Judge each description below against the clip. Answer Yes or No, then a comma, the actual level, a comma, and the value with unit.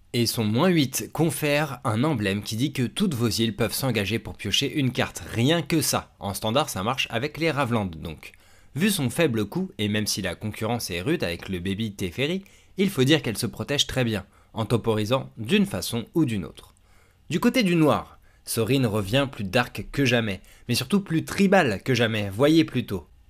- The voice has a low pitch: Yes, low, 115 Hz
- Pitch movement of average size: No, wide, 6.2 semitones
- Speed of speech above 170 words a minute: Yes, average, 200 wpm